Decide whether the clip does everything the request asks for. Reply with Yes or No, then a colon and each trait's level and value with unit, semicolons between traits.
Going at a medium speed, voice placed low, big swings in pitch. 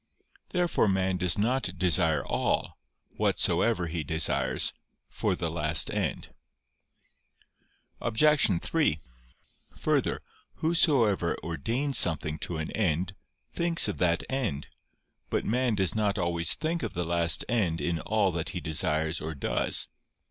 No: slow, 125 wpm; very low, 90 Hz; wide, 6.2 semitones